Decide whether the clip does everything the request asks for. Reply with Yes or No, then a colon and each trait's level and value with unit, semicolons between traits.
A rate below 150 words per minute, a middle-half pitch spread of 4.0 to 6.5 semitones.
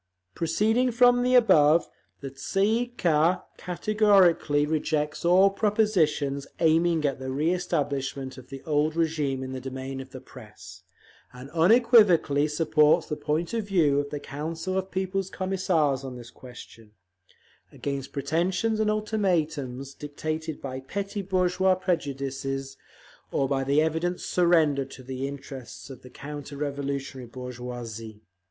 Yes: slow, 135 wpm; average, 5.1 semitones